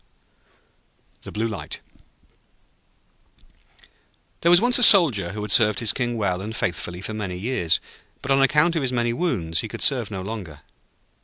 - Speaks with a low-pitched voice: Yes, low, 110 Hz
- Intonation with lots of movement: Yes, wide, 6.0 semitones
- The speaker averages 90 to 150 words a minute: No, average, 170 wpm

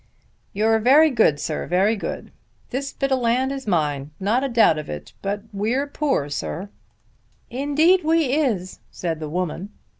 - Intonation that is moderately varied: No, wide, 7.3 semitones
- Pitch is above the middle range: Yes, high, 220 Hz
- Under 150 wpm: No, average, 160 wpm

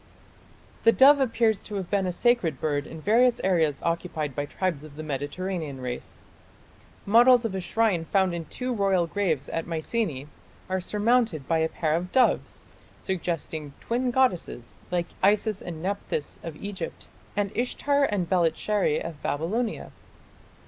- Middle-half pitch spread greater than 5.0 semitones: Yes, wide, 5.5 semitones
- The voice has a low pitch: No, medium, 185 Hz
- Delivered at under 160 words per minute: Yes, average, 150 wpm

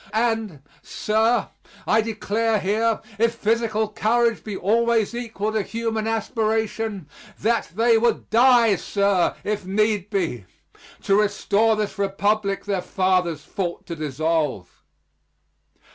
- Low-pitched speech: No, high, 215 Hz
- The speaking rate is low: Yes, slow, 115 wpm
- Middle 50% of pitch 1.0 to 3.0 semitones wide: Yes, narrow, 2.4 semitones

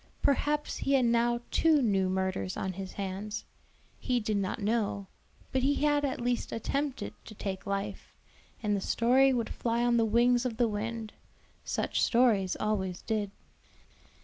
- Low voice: No, high, 230 Hz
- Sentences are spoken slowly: No, average, 160 wpm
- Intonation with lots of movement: No, average, 3.7 semitones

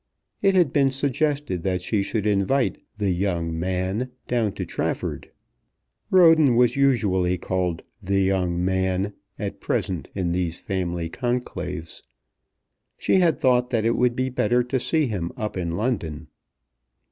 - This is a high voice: No, low, 100 Hz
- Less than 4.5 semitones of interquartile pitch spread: No, wide, 5.6 semitones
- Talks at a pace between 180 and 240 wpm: No, average, 145 wpm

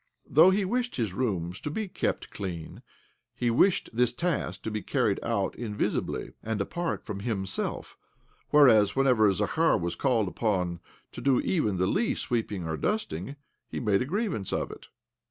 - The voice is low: Yes, low, 115 Hz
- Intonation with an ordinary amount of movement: No, wide, 7.4 semitones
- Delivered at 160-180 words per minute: Yes, average, 165 wpm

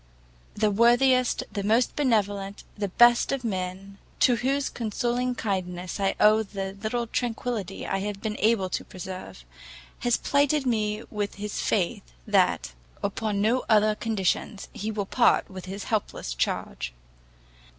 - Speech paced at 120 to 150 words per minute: Yes, average, 140 wpm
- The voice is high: Yes, high, 210 Hz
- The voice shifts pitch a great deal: No, average, 3.5 semitones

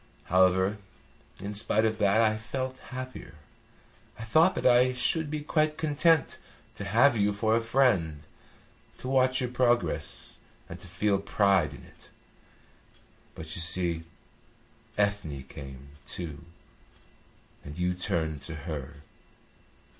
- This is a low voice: Yes, low, 105 Hz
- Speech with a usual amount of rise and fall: No, wide, 7.2 semitones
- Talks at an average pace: No, slow, 130 wpm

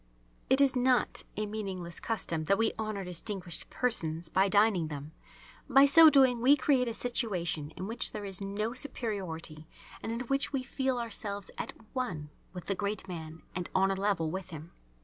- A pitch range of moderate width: No, wide, 5.9 semitones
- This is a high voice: Yes, high, 200 Hz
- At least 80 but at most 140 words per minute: No, average, 180 wpm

